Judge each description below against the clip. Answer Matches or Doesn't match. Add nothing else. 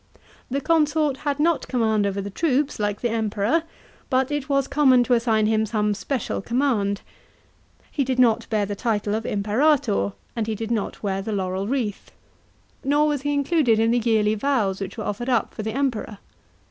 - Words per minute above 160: Matches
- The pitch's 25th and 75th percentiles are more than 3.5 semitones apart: Matches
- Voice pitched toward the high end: Matches